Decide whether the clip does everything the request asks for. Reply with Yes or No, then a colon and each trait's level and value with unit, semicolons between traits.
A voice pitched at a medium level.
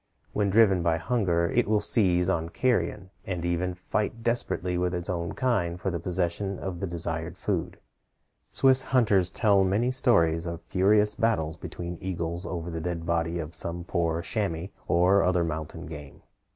No: very low, 90 Hz